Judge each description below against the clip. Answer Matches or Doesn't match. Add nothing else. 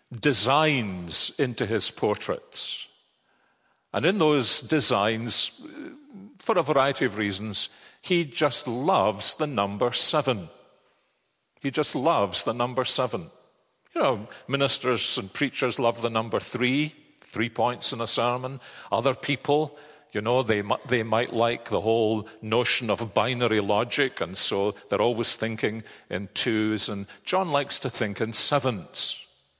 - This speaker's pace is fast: Doesn't match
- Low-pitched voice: Matches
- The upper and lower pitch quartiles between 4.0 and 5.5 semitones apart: Matches